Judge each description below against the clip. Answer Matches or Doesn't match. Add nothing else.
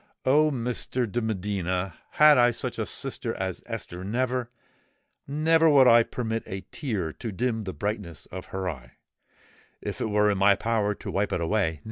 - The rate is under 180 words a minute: Matches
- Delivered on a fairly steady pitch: Doesn't match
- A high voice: Doesn't match